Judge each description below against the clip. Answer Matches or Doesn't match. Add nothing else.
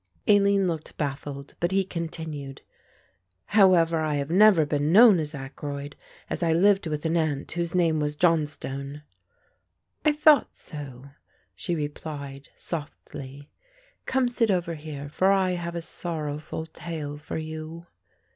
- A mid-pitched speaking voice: Matches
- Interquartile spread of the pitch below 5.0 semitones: Matches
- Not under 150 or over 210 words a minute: Doesn't match